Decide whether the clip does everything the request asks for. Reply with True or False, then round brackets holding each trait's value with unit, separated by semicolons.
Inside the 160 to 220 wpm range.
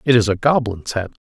False (235 wpm)